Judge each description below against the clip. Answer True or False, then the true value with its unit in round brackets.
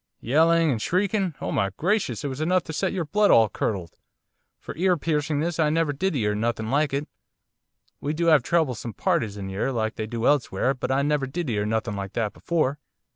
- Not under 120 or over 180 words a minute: False (205 wpm)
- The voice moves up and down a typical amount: False (6.7 semitones)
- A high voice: False (145 Hz)